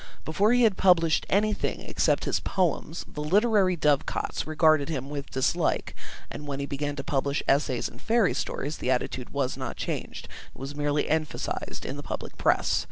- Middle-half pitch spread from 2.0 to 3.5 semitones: No, average, 4.3 semitones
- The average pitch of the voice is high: No, medium, 150 Hz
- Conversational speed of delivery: Yes, average, 175 wpm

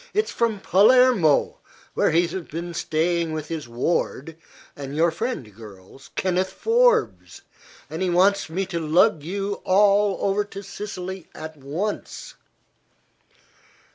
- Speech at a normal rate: No, slow, 130 wpm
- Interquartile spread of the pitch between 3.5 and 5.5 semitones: Yes, average, 4.2 semitones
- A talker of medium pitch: Yes, medium, 180 Hz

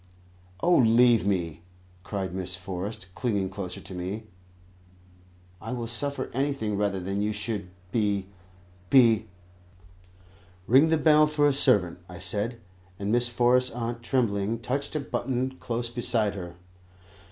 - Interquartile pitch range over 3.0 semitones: Yes, average, 4.5 semitones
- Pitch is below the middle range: Yes, low, 110 Hz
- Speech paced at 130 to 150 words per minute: Yes, average, 140 wpm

